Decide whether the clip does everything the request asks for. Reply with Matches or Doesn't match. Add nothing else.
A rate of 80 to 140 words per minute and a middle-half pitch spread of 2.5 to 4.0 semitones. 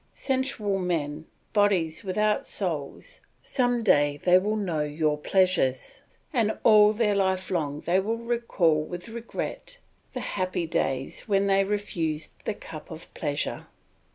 Doesn't match